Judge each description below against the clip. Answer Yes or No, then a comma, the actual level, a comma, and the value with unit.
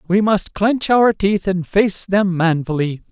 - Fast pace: No, average, 175 wpm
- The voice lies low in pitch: No, high, 190 Hz